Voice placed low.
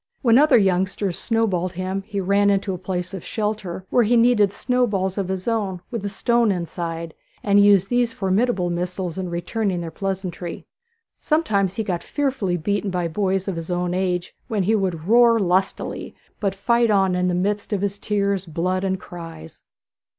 No: high, 195 Hz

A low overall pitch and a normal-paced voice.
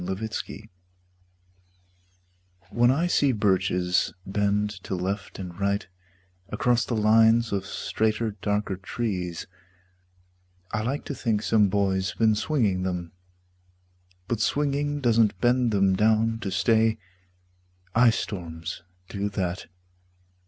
No: low, 105 Hz; slow, 110 wpm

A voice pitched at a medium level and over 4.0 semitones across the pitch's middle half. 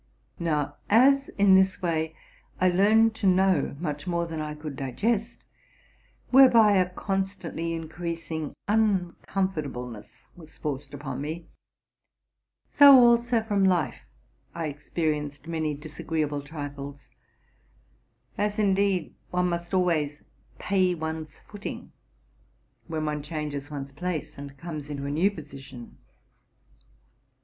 Yes: medium, 165 Hz; average, 4.6 semitones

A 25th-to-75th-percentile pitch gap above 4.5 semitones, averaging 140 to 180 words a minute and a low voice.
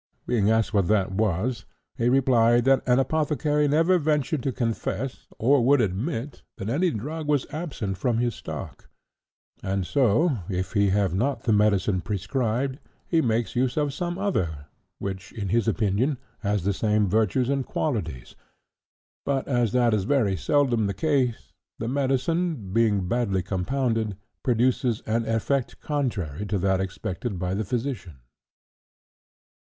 Yes: average, 5.3 semitones; average, 145 wpm; low, 115 Hz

